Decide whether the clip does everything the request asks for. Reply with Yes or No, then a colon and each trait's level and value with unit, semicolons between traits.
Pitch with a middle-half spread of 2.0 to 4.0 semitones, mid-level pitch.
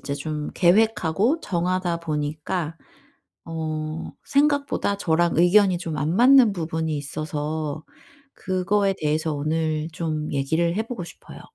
Yes: average, 3.5 semitones; medium, 165 Hz